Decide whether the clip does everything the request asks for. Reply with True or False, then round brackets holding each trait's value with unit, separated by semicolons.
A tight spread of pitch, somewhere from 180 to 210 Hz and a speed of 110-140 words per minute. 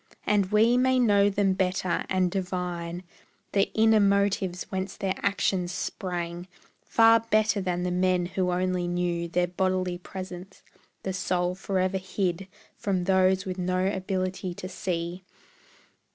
True (1.6 semitones; 185 Hz; 135 wpm)